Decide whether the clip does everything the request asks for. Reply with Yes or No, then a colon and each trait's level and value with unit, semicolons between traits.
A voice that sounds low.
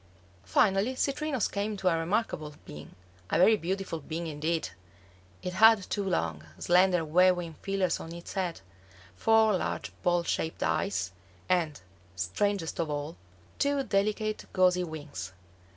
No: medium, 180 Hz